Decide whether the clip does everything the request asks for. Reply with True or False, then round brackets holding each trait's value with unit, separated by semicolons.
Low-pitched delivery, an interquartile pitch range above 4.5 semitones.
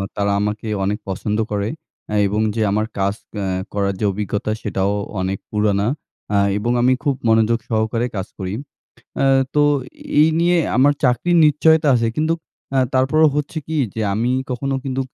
True (110 Hz; 5.0 semitones)